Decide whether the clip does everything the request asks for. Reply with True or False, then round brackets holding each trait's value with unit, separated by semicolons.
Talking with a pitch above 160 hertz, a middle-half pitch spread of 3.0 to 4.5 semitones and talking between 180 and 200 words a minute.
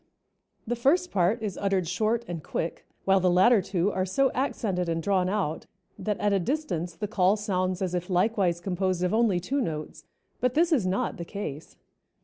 True (190 Hz; 3.6 semitones; 190 wpm)